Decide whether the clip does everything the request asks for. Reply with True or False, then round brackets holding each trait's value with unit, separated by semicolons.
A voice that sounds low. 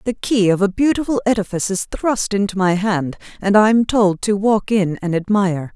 False (205 Hz)